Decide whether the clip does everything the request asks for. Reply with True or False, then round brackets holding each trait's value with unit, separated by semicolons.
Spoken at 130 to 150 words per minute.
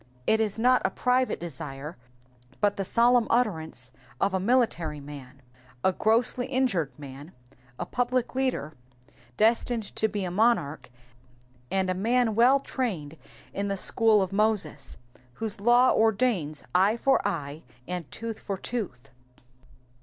True (140 wpm)